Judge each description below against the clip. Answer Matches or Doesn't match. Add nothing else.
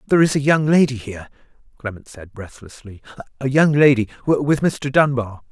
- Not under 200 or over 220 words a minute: Doesn't match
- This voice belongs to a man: Matches